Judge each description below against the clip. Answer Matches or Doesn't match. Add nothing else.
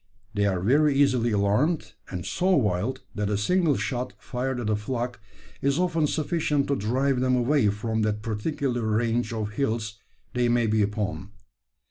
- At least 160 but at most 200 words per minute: Matches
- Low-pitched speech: Matches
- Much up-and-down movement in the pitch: Doesn't match